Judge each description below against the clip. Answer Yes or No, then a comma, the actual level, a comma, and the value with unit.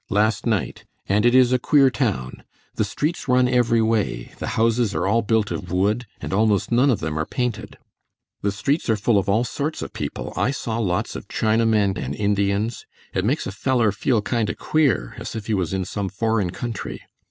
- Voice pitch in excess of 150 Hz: No, low, 110 Hz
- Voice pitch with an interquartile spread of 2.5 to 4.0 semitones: Yes, average, 3.4 semitones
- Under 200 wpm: No, fast, 205 wpm